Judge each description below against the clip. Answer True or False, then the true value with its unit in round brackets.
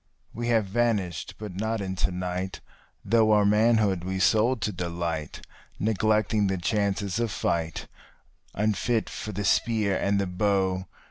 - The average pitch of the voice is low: True (100 Hz)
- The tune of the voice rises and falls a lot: False (2.7 semitones)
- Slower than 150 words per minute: True (140 wpm)